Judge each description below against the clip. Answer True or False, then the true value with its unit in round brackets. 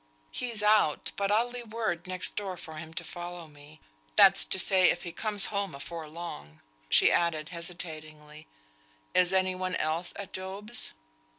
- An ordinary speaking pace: True (165 wpm)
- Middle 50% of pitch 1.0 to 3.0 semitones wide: False (4.0 semitones)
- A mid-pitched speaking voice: True (175 Hz)